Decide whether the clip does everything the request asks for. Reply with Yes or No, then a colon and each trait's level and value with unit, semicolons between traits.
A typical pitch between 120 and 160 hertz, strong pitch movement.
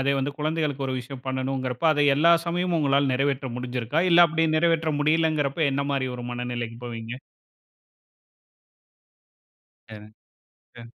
No: medium, 140 Hz; average, 3.8 semitones